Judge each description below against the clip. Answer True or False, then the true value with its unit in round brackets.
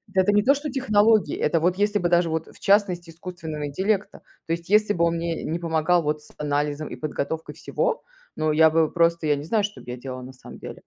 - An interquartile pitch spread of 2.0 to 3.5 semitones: False (4.7 semitones)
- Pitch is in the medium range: True (170 Hz)